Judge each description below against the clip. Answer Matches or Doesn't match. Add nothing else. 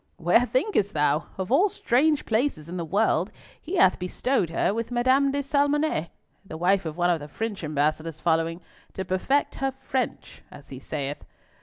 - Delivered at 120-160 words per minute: Doesn't match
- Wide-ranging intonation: Matches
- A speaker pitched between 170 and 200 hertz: Matches